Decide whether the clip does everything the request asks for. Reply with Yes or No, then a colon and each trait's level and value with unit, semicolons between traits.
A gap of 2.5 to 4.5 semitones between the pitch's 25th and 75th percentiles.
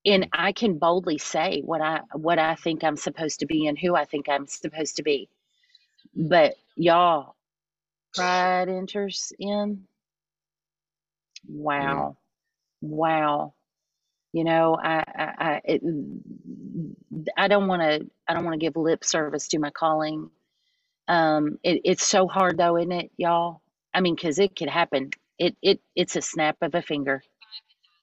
Yes: average, 2.8 semitones